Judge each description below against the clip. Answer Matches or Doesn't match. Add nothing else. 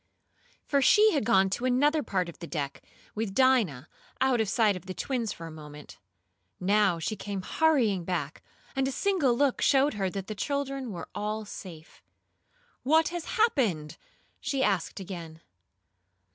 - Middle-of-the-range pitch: Doesn't match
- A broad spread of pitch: Matches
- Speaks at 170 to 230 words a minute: Doesn't match